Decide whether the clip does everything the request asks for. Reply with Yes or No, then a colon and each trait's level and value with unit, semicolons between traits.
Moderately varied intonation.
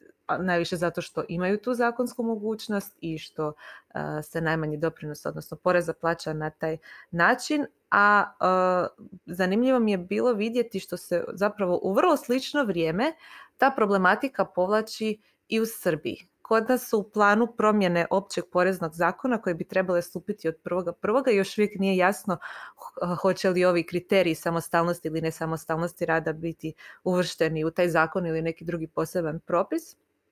Yes: average, 4.6 semitones